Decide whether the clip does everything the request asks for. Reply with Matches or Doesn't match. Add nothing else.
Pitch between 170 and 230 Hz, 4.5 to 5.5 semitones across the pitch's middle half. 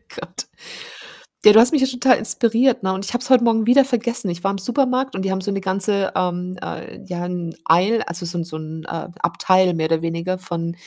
Matches